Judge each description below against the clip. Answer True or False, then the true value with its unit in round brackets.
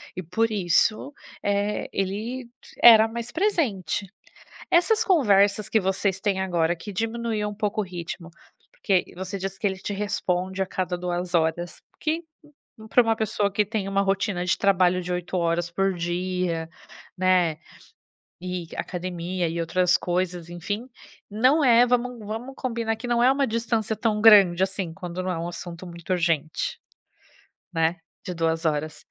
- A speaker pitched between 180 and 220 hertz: True (190 Hz)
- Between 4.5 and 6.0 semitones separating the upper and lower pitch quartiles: False (4.0 semitones)